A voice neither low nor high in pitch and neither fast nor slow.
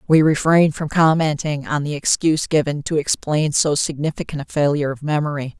Yes: medium, 150 Hz; average, 170 wpm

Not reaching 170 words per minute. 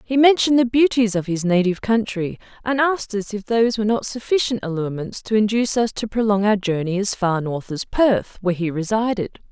No: average, 200 wpm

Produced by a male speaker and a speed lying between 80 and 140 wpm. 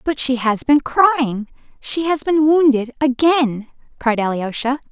No: female; slow, 135 wpm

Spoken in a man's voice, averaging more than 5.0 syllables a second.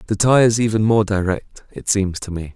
Yes: male; 5.2 syllables/s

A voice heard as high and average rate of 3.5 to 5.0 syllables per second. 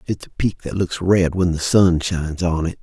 No: very low, 85 Hz; 4.9 syllables/s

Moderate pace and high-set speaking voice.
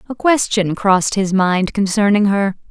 Yes: average, 155 wpm; high, 200 Hz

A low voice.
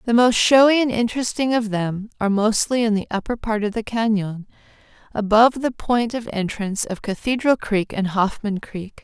No: high, 220 Hz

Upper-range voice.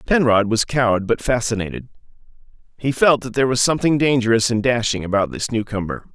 No: low, 120 Hz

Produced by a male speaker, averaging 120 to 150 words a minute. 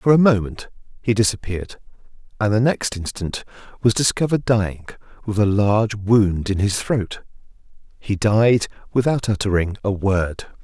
Yes: male; average, 140 wpm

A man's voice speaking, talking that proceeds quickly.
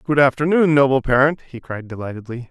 No: male; average, 170 wpm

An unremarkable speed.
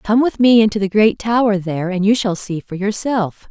No: fast, 240 wpm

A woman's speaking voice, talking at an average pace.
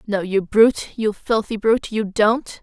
Yes: female; average, 185 wpm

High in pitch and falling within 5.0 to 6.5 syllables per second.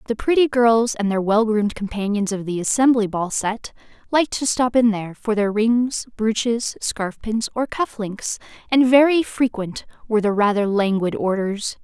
No: high, 220 Hz; 4.7 syllables/s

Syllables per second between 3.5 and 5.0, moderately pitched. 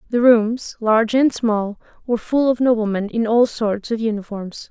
No: 4.7 syllables/s; high, 225 Hz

